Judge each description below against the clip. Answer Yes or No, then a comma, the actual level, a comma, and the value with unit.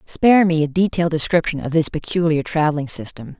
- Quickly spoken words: No, average, 175 wpm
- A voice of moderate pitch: Yes, medium, 160 Hz